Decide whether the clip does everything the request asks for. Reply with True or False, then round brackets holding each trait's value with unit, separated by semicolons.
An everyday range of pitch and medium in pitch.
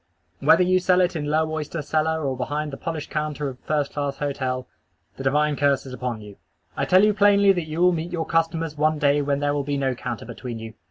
True (3.1 semitones; 150 Hz)